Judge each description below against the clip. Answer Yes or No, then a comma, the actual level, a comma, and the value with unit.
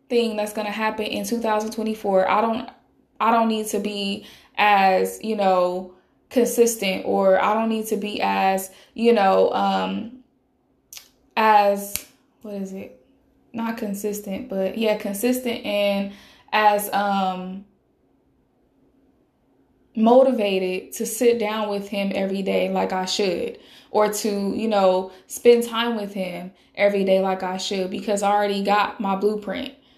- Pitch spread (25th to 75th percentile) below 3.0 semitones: Yes, narrow, 2.6 semitones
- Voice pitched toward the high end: Yes, high, 205 Hz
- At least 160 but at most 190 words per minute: No, average, 140 wpm